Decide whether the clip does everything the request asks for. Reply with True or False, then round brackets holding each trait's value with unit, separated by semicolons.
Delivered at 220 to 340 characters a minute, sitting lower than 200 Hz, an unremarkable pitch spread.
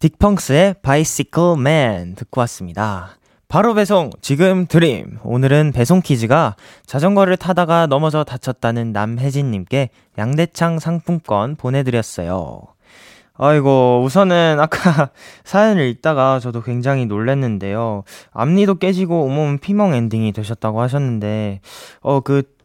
False (290 characters per minute; 140 Hz; 6.2 semitones)